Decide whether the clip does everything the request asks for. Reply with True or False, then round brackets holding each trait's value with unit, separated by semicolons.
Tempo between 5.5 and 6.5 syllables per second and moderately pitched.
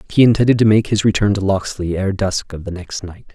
False (5.7 syllables/s; 100 Hz)